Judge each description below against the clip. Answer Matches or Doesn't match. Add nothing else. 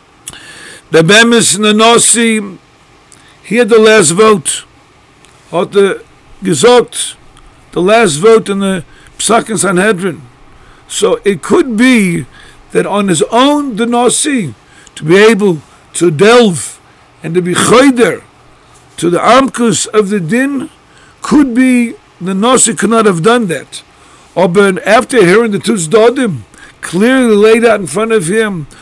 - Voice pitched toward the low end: Doesn't match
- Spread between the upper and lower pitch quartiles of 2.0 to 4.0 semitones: Doesn't match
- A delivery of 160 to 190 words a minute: Doesn't match